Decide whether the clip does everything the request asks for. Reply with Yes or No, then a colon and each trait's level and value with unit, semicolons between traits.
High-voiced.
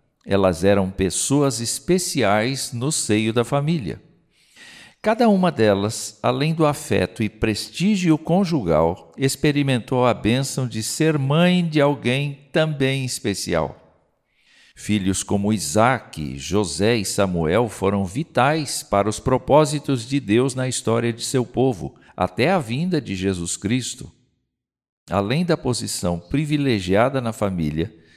No: low, 125 Hz